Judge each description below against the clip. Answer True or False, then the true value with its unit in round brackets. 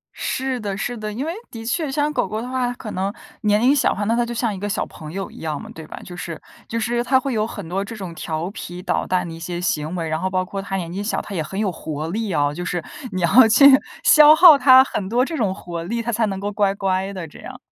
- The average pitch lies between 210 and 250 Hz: False (200 Hz)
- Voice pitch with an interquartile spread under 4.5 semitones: False (5.1 semitones)